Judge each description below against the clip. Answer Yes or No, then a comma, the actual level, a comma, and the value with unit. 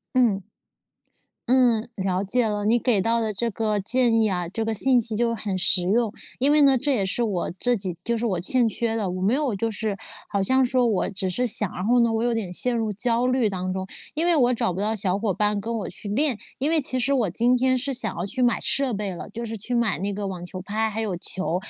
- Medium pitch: No, high, 225 Hz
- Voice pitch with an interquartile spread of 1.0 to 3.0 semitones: No, average, 3.8 semitones